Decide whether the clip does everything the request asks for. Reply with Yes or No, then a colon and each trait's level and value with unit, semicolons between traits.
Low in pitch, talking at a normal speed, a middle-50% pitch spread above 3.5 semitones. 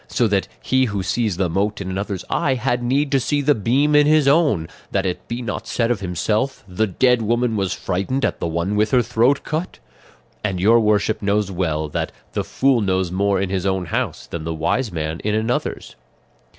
No: low, 105 Hz; fast, 210 wpm; average, 4.8 semitones